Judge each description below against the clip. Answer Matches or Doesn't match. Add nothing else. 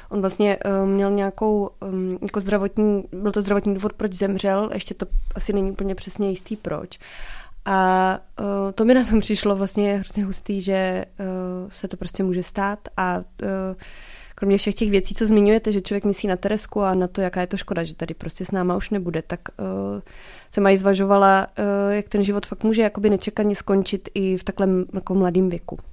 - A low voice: Doesn't match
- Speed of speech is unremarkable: Doesn't match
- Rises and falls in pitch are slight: Matches